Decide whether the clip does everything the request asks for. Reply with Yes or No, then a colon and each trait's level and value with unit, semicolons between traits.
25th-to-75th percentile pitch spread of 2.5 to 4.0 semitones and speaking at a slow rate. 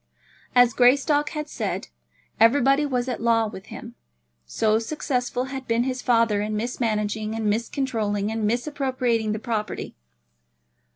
Yes: average, 3.1 semitones; slow, 130 wpm